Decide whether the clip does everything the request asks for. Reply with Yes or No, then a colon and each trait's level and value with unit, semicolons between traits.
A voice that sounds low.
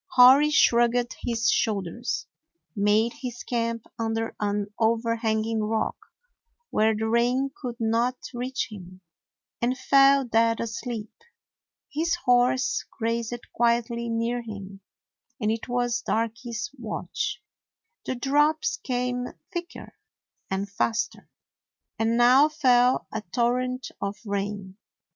No: high, 235 Hz